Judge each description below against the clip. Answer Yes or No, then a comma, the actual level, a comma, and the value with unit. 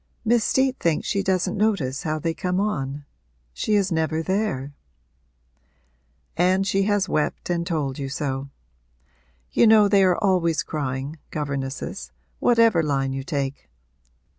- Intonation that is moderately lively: No, wide, 6.0 semitones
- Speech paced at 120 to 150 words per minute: Yes, average, 140 wpm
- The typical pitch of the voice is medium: Yes, medium, 165 Hz